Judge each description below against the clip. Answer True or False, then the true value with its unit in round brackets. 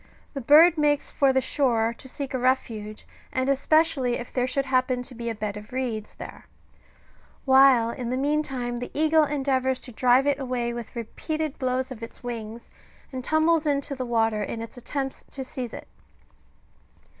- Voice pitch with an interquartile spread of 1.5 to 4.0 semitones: True (2.8 semitones)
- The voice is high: True (255 Hz)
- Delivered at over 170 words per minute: True (180 wpm)